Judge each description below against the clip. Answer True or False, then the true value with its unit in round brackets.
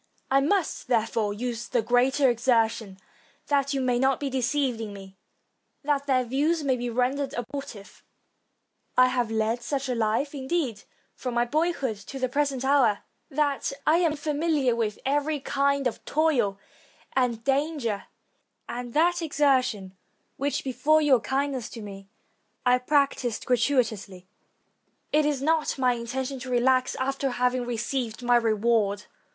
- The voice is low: False (255 Hz)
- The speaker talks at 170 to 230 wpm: False (150 wpm)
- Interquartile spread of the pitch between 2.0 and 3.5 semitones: True (3.2 semitones)